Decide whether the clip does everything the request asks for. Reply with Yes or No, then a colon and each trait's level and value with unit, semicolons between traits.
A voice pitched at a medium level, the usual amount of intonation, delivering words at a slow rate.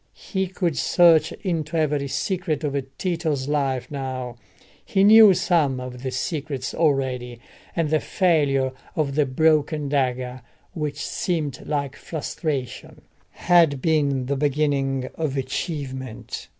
Yes: medium, 145 Hz; average, 3.4 semitones; slow, 125 wpm